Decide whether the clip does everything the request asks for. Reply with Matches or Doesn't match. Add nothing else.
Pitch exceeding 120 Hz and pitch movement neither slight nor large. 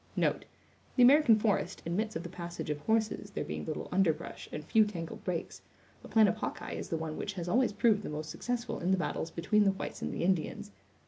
Matches